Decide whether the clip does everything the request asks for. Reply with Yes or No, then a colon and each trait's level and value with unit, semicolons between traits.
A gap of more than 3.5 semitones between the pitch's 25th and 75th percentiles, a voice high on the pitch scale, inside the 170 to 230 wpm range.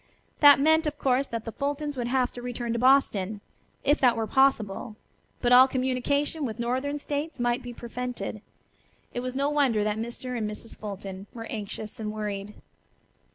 Yes: average, 3.9 semitones; high, 245 Hz; average, 175 wpm